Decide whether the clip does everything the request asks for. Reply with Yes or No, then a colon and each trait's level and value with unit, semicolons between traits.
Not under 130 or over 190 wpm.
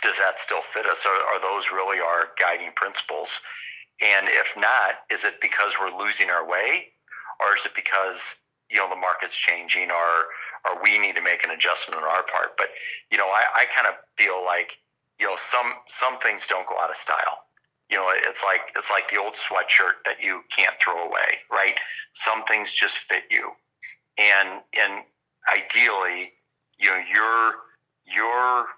Yes: average, 180 wpm